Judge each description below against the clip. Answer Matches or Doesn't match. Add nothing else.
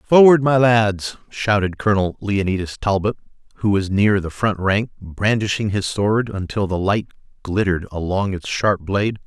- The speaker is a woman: Doesn't match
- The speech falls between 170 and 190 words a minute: Doesn't match